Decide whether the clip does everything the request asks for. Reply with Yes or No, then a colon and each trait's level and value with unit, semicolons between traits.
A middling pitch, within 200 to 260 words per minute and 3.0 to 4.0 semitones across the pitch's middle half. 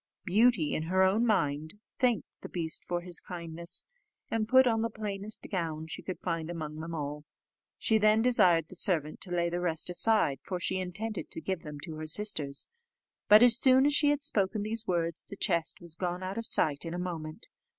No: medium, 180 Hz; fast, 205 wpm; average, 4.7 semitones